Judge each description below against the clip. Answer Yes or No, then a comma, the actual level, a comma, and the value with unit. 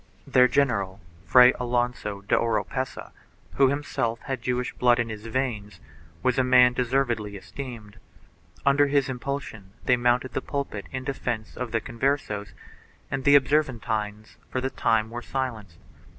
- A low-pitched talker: Yes, low, 125 Hz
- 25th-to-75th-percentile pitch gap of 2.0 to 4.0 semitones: Yes, average, 3.3 semitones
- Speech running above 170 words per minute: No, average, 145 wpm